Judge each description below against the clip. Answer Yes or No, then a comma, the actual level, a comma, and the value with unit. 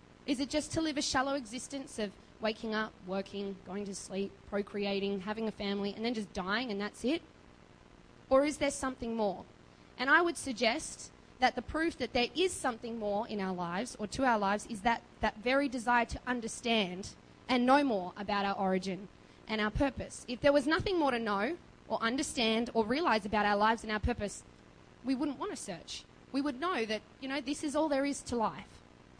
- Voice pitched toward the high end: Yes, high, 230 Hz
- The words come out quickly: Yes, fast, 210 wpm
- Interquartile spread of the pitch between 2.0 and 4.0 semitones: No, average, 5.1 semitones